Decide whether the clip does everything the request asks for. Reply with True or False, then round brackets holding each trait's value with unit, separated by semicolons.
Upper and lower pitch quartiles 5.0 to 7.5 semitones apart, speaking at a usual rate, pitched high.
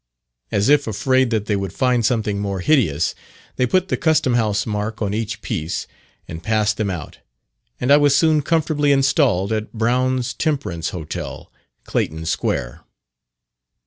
False (5.3 semitones; 150 wpm; 110 Hz)